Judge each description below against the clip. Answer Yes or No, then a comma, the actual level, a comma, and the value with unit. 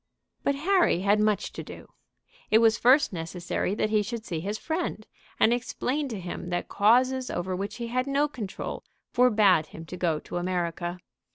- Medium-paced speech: Yes, average, 180 wpm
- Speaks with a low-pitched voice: No, high, 215 Hz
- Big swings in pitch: Yes, wide, 5.8 semitones